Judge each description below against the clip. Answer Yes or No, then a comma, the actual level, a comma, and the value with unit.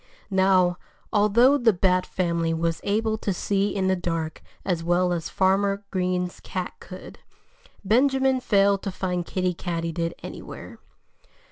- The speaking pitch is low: No, medium, 185 Hz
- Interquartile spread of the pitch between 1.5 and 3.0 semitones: Yes, narrow, 2.4 semitones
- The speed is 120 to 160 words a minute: Yes, slow, 135 wpm